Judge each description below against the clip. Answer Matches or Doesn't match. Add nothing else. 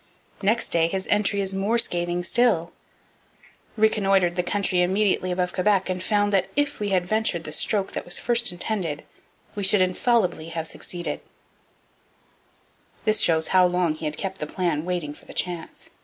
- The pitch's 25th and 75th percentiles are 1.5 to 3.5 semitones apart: Matches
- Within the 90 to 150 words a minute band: Doesn't match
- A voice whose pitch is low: Doesn't match